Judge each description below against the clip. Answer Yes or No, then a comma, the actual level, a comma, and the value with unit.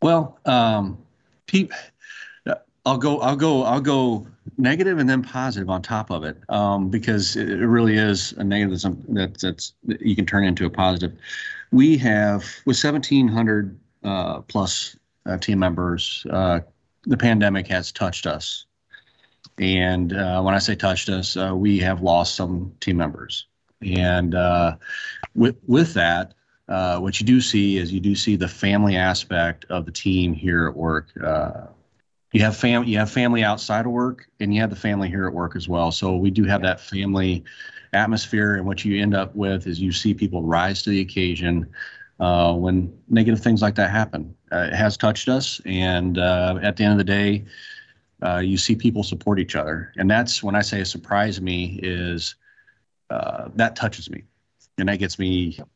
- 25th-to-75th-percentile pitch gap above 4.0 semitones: No, average, 3.4 semitones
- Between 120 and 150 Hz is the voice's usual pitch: No, low, 100 Hz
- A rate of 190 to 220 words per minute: No, average, 180 wpm